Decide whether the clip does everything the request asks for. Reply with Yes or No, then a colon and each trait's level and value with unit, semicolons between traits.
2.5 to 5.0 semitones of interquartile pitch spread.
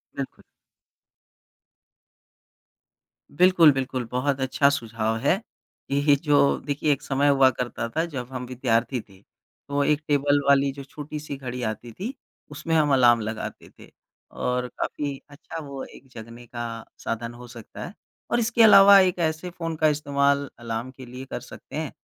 Yes: average, 3.3 semitones